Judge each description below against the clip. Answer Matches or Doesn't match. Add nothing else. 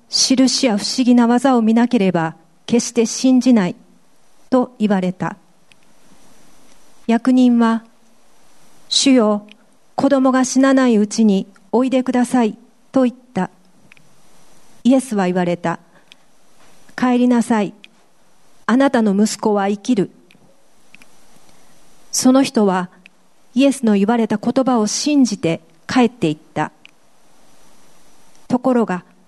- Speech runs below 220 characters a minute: Matches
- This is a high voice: Matches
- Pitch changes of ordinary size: Matches